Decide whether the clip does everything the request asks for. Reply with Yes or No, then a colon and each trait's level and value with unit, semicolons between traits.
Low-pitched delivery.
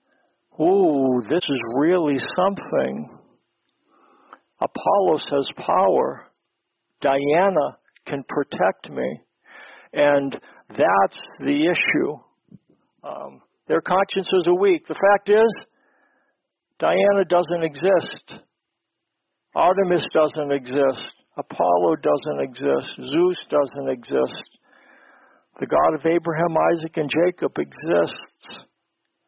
No: medium, 165 Hz